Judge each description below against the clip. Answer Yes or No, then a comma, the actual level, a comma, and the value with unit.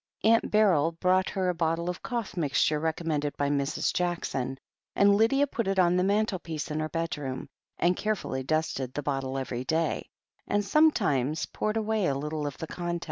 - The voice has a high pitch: No, medium, 165 Hz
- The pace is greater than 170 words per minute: Yes, average, 180 wpm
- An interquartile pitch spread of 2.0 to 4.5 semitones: No, average, 5.1 semitones